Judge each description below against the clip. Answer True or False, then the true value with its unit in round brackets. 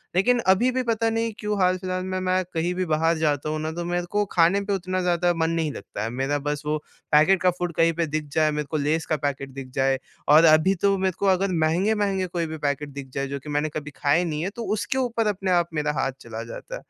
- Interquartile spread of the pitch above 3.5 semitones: True (3.9 semitones)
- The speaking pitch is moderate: True (170 Hz)